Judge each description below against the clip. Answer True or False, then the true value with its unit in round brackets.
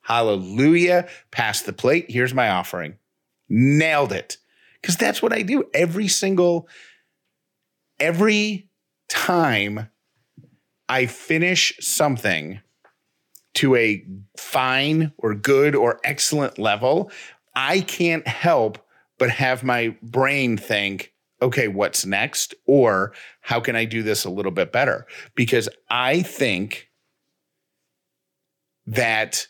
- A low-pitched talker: True (130 Hz)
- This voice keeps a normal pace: False (110 wpm)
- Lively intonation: True (7.9 semitones)